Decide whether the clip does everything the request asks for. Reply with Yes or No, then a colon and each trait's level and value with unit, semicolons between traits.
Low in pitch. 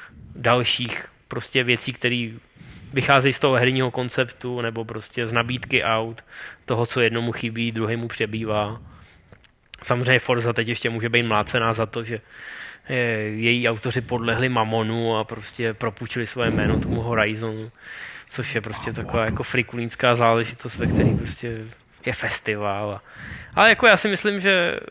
Yes: low, 115 Hz